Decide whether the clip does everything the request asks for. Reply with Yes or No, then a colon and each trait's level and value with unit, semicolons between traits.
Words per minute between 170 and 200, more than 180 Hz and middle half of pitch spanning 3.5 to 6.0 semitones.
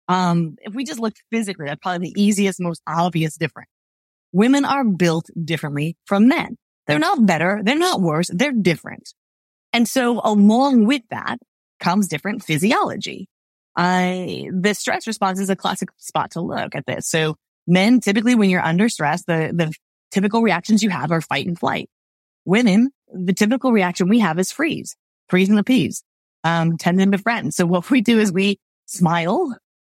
Yes: average, 175 wpm; high, 190 Hz; average, 4.8 semitones